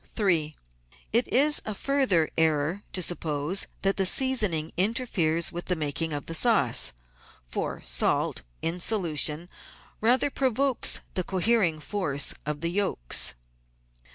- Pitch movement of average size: No, wide, 5.9 semitones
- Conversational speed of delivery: No, slow, 130 wpm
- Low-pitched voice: No, medium, 175 Hz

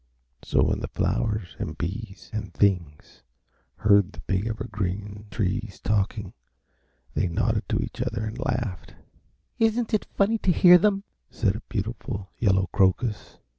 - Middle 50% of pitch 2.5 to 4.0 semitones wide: Yes, average, 3.4 semitones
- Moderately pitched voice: No, low, 105 Hz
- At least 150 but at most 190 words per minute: No, average, 140 wpm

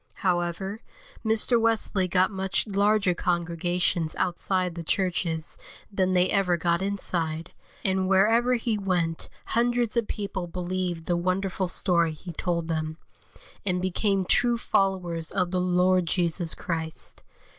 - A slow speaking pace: Yes, slow, 130 wpm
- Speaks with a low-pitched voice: No, medium, 185 Hz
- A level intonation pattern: Yes, narrow, 2.3 semitones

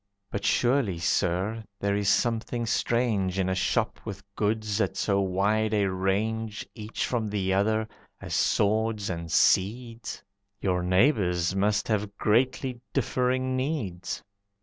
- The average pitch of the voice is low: Yes, low, 105 Hz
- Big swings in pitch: No, average, 2.9 semitones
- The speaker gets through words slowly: Yes, slow, 130 wpm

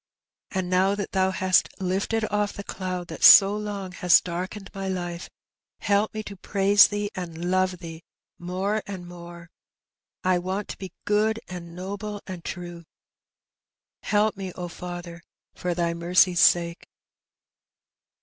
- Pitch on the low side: No, medium, 185 Hz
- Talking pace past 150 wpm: No, average, 145 wpm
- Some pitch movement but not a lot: No, narrow, 2.3 semitones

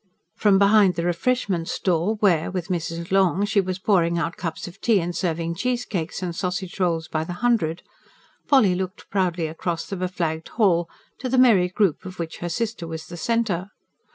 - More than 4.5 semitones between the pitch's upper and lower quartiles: No, average, 3.2 semitones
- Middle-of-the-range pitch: Yes, medium, 180 Hz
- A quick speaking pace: No, average, 180 wpm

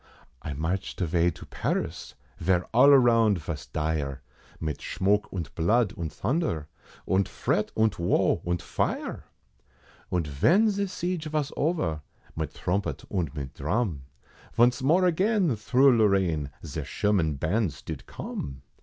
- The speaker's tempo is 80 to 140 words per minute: Yes, slow, 135 wpm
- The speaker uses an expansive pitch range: Yes, wide, 7.9 semitones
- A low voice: Yes, very low, 95 Hz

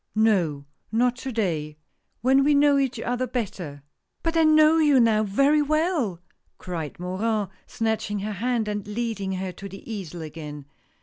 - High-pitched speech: Yes, high, 220 Hz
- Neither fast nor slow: Yes, average, 160 wpm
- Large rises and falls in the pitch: Yes, wide, 6.1 semitones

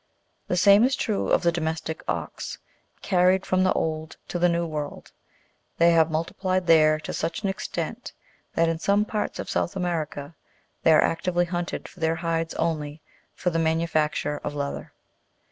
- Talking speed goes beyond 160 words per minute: Yes, average, 170 wpm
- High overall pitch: No, medium, 165 Hz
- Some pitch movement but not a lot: No, narrow, 2.2 semitones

